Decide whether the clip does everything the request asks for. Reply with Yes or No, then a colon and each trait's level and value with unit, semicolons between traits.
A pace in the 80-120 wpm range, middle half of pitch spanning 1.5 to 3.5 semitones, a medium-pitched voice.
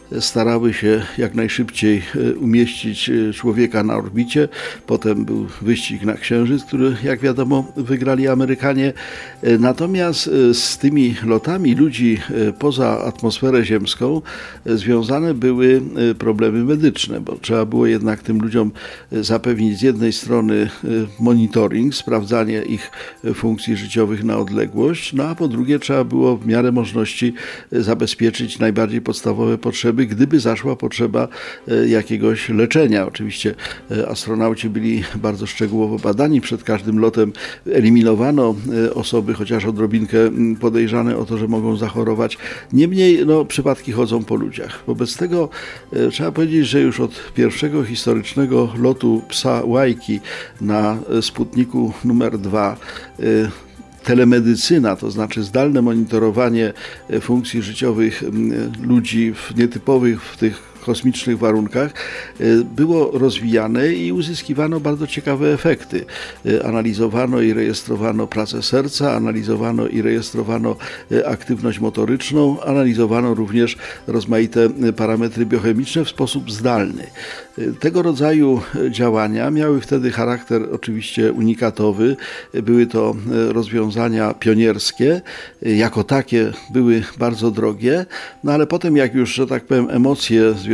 No: average, 115 wpm; narrow, 2.6 semitones; low, 115 Hz